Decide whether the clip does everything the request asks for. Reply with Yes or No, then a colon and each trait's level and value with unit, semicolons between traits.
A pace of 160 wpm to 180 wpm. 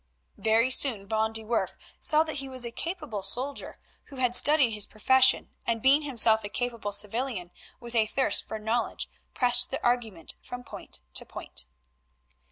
Yes: average, 170 wpm